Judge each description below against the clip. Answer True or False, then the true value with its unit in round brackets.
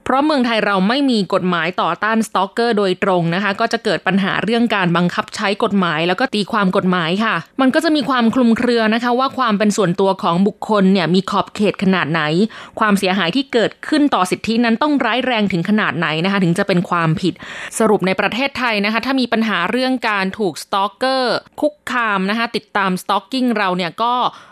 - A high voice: True (210 Hz)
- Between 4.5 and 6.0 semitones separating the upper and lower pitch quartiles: False (3.9 semitones)